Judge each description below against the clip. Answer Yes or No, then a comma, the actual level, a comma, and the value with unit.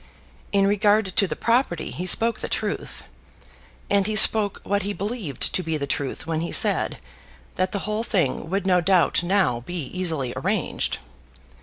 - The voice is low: No, high, 190 Hz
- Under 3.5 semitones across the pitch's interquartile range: No, average, 3.8 semitones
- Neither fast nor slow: Yes, average, 170 wpm